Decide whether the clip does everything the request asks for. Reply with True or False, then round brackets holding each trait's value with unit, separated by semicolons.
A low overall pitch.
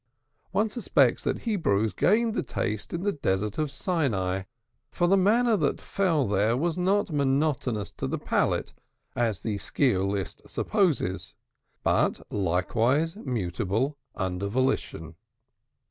True (130 Hz)